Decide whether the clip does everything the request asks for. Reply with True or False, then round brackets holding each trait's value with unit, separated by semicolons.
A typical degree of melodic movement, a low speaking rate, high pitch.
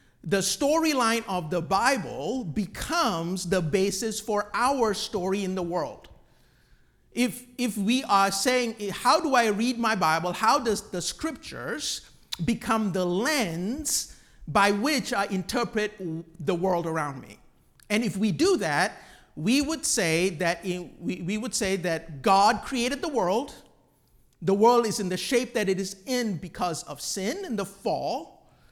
False (4.6 semitones; 160 wpm; 205 Hz)